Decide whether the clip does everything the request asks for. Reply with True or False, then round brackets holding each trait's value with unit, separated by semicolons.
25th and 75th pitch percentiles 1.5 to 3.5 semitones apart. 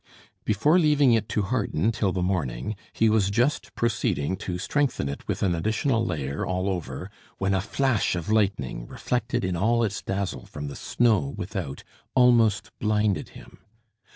False (4.6 semitones)